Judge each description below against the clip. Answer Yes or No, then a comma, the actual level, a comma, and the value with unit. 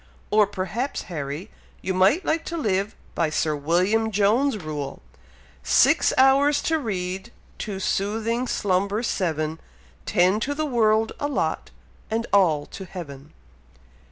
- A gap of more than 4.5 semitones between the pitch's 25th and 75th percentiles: Yes, average, 4.9 semitones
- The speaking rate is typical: No, slow, 130 wpm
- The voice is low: No, high, 200 Hz